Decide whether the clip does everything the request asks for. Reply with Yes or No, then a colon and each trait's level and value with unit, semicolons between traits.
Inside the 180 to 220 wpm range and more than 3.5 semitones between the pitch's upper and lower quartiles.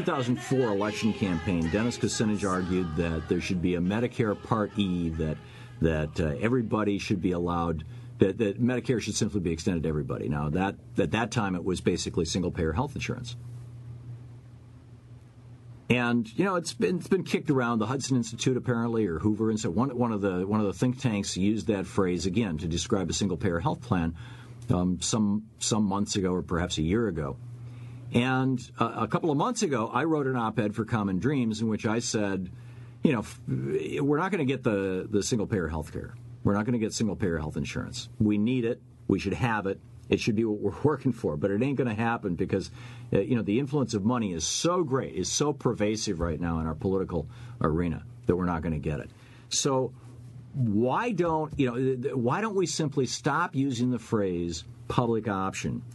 Yes: fast, 205 wpm; average, 4.1 semitones